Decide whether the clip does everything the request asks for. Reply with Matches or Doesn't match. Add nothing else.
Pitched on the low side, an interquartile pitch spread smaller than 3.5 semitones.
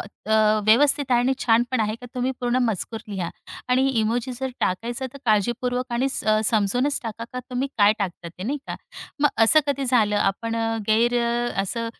Doesn't match